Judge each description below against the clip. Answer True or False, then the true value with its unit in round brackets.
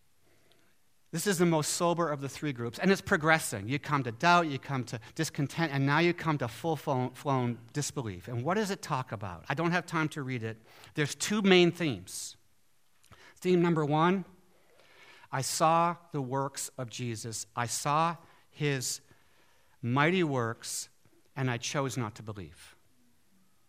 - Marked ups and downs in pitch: True (5.7 semitones)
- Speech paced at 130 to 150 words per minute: False (165 wpm)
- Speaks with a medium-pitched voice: True (145 Hz)